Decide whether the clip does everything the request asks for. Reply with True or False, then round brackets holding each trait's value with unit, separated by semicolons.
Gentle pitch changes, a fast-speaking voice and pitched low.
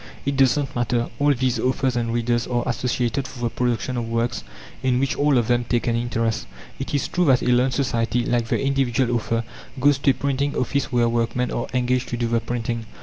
True (2.0 semitones; 220 wpm; 125 Hz)